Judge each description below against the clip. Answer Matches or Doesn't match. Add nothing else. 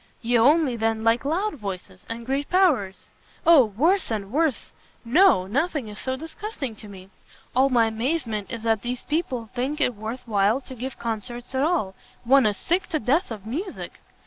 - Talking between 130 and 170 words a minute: Doesn't match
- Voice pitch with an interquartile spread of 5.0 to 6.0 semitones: Matches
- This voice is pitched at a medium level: Doesn't match